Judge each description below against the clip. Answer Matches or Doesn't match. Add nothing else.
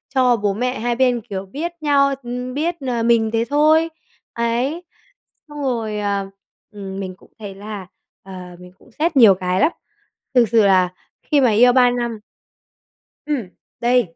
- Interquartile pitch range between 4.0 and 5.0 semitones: Matches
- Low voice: Doesn't match